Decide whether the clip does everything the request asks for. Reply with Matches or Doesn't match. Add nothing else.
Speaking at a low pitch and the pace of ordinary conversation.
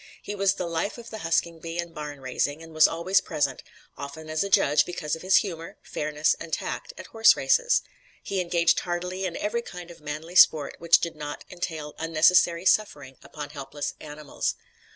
Doesn't match